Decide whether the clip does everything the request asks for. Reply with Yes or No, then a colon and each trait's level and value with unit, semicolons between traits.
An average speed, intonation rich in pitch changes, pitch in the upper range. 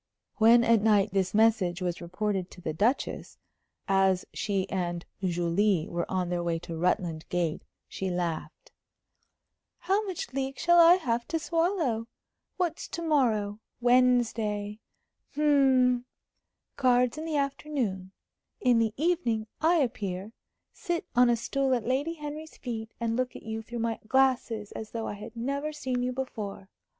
Yes: average, 150 wpm; wide, 5.7 semitones; high, 230 Hz